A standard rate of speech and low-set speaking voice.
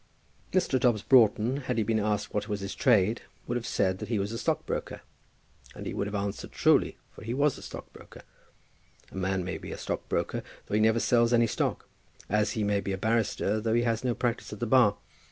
No: fast, 220 wpm; low, 110 Hz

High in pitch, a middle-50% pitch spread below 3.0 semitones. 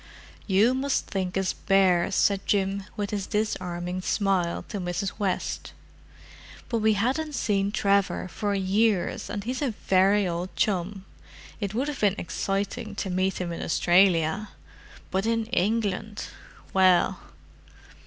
Yes: high, 195 Hz; narrow, 2.4 semitones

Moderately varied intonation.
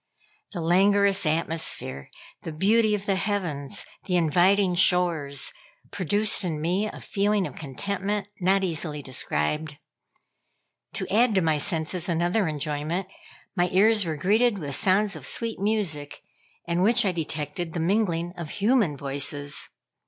Yes: average, 4.4 semitones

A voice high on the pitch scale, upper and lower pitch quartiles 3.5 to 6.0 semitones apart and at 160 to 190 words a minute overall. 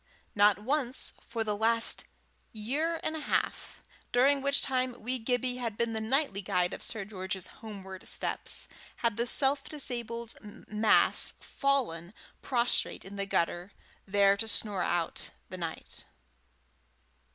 No: high, 225 Hz; average, 4.2 semitones; average, 140 wpm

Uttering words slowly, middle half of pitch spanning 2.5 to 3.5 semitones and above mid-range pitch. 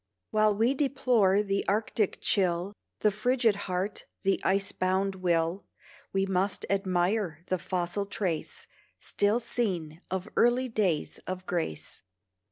Yes: slow, 125 wpm; average, 2.8 semitones; high, 195 Hz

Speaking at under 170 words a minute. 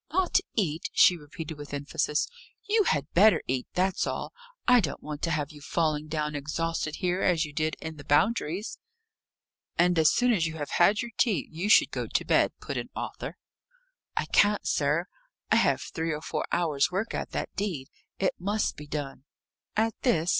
No: average, 190 wpm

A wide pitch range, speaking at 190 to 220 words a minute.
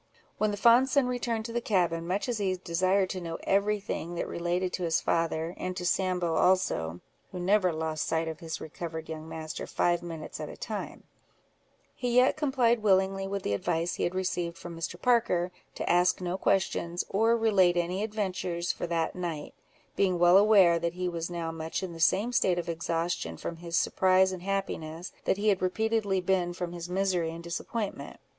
No: average, 2.7 semitones; average, 195 wpm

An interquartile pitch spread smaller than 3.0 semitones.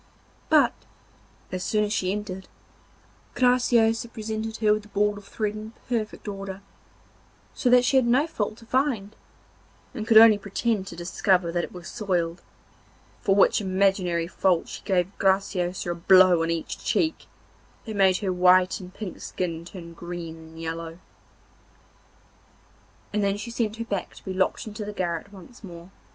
No: average, 3.3 semitones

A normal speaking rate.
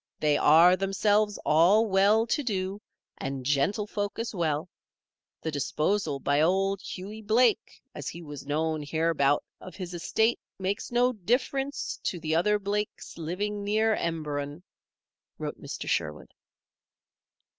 No: slow, 130 wpm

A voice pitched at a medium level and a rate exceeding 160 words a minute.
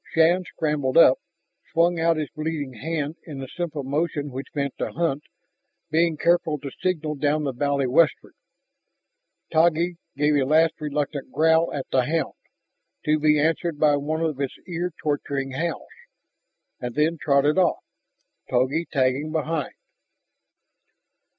No: medium, 150 Hz; average, 140 wpm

